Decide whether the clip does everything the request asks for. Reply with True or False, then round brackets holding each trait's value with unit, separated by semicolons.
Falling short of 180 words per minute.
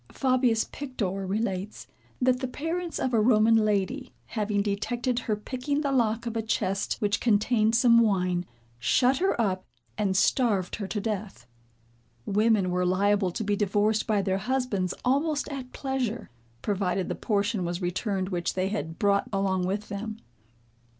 True (155 wpm)